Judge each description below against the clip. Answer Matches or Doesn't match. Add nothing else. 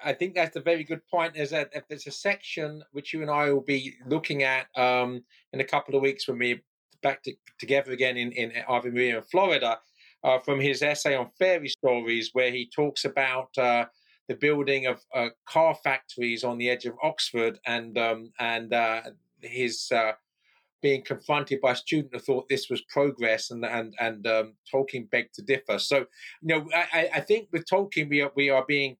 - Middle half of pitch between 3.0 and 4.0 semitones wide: Matches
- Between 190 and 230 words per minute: Matches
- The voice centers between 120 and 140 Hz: Matches